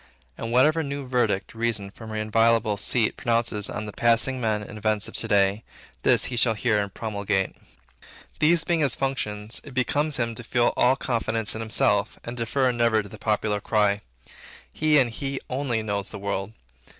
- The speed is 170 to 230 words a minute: Yes, average, 185 wpm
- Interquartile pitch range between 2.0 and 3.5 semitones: Yes, average, 3.2 semitones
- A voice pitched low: Yes, low, 115 Hz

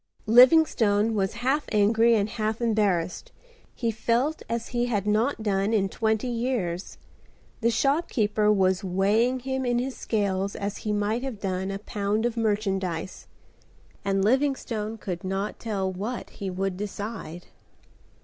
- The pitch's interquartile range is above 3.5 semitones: No, average, 3.2 semitones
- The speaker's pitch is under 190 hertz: No, high, 215 Hz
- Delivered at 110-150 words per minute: Yes, average, 140 wpm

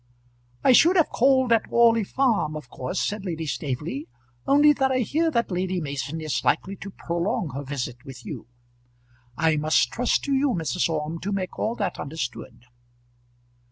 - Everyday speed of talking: Yes, average, 170 wpm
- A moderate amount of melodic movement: No, wide, 8.0 semitones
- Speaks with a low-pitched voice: No, medium, 180 Hz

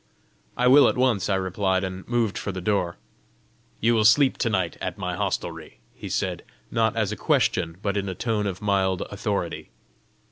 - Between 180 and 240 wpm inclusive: Yes, average, 185 wpm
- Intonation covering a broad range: No, average, 3.4 semitones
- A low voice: Yes, low, 100 Hz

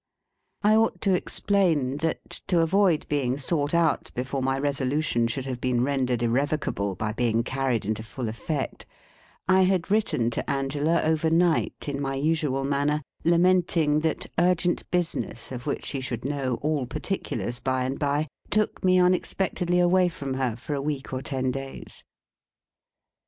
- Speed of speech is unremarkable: Yes, average, 155 wpm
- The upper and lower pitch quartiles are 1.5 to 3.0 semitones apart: No, average, 4.6 semitones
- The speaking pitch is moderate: Yes, medium, 145 Hz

